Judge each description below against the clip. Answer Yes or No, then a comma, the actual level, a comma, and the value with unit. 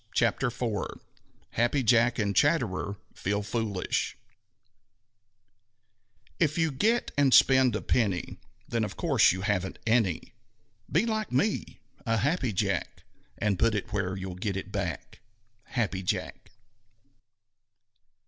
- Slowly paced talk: Yes, slow, 120 wpm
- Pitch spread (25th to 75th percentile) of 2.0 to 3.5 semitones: No, average, 4.8 semitones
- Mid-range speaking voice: No, low, 115 Hz